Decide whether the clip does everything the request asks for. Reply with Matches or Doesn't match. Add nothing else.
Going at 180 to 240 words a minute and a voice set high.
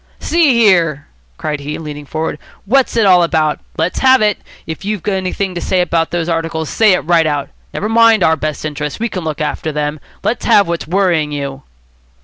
Doesn't match